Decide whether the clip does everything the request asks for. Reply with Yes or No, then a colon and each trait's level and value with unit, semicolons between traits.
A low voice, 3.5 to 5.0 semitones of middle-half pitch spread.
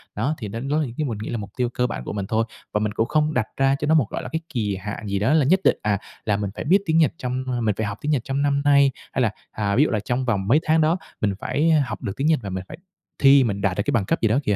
No: low, 120 Hz; wide, 5.6 semitones